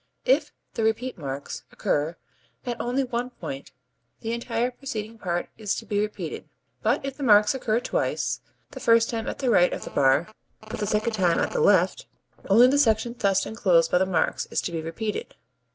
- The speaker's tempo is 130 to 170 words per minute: No, average, 195 wpm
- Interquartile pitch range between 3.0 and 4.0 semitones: No, average, 4.8 semitones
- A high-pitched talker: Yes, high, 220 Hz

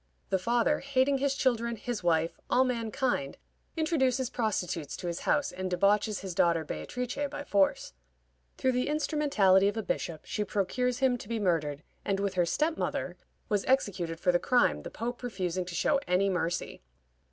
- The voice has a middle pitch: No, high, 210 Hz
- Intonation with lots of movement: Yes, wide, 6.0 semitones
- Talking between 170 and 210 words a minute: Yes, average, 175 wpm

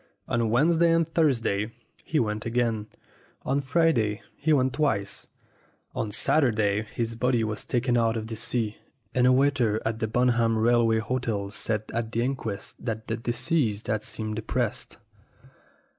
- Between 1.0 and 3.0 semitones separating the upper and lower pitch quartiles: Yes, average, 2.7 semitones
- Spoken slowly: No, average, 155 wpm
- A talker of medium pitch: No, low, 115 Hz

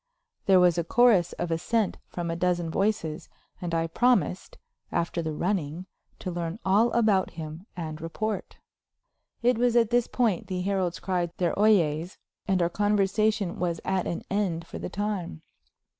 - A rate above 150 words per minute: Yes, average, 160 wpm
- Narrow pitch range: No, average, 3.7 semitones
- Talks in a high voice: No, medium, 180 Hz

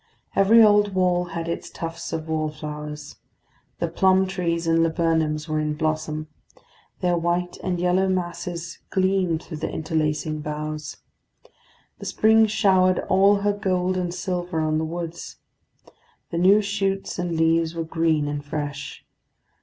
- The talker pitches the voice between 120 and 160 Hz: No, medium, 170 Hz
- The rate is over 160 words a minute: No, average, 140 wpm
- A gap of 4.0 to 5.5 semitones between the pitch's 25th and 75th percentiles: No, average, 3.0 semitones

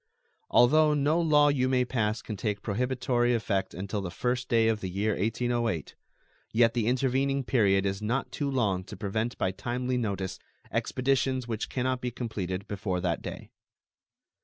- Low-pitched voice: Yes, low, 115 Hz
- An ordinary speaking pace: Yes, average, 165 wpm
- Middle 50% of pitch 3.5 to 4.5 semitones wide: Yes, average, 4.1 semitones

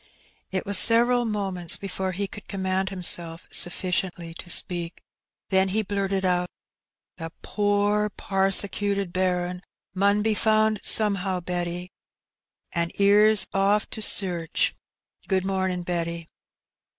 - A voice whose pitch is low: No, high, 190 Hz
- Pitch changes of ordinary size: No, narrow, 2.3 semitones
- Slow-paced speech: Yes, slow, 125 wpm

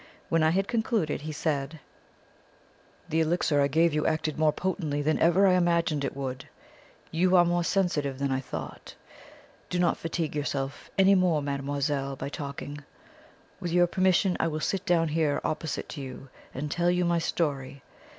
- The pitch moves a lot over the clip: No, average, 3.5 semitones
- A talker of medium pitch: Yes, medium, 155 Hz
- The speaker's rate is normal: Yes, average, 170 wpm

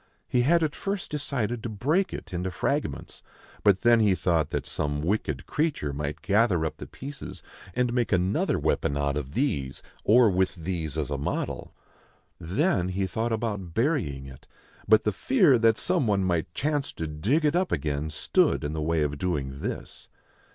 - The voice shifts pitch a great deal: Yes, wide, 8.2 semitones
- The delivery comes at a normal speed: Yes, average, 180 wpm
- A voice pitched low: Yes, very low, 95 Hz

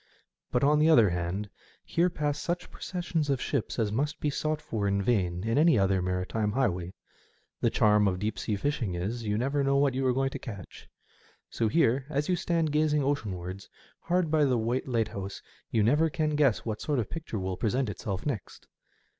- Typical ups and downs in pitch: No, wide, 6.3 semitones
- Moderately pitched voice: No, low, 125 Hz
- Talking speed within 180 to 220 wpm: Yes, average, 195 wpm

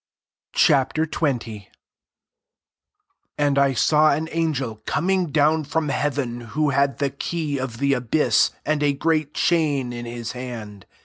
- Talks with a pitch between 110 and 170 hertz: Yes, medium, 140 Hz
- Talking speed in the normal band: Yes, average, 150 wpm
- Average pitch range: Yes, average, 3.6 semitones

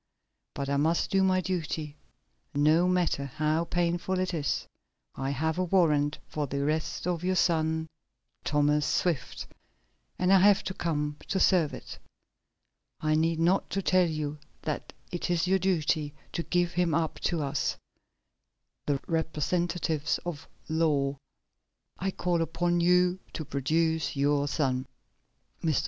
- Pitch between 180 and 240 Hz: No, medium, 160 Hz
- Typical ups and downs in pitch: Yes, average, 3.1 semitones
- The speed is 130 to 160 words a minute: Yes, average, 140 wpm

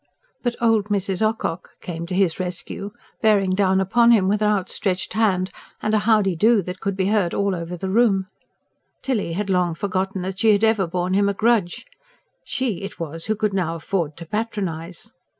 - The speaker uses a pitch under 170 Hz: No, high, 195 Hz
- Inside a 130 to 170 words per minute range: No, average, 190 wpm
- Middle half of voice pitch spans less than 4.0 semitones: Yes, average, 2.9 semitones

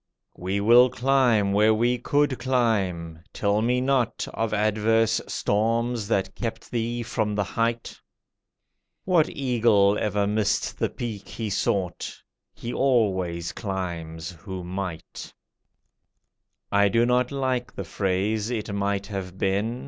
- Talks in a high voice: No, low, 110 Hz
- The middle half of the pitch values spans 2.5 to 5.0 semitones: Yes, average, 3.3 semitones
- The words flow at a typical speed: No, slow, 125 wpm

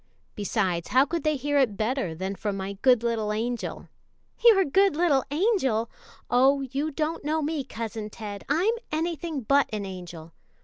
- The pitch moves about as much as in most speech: No, wide, 6.4 semitones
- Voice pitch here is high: Yes, very high, 260 Hz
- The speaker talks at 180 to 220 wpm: No, average, 165 wpm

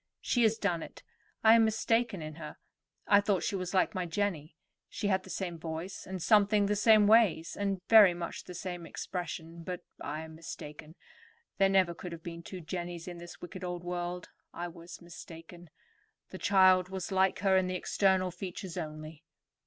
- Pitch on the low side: No, medium, 180 Hz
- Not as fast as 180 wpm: No, average, 185 wpm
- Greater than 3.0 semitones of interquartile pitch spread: No, narrow, 2.6 semitones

